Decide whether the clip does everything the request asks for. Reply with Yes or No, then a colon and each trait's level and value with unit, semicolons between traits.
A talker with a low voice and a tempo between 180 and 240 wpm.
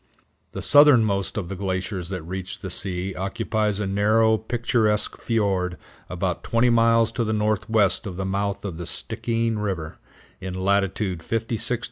No: low, 100 Hz; average, 155 wpm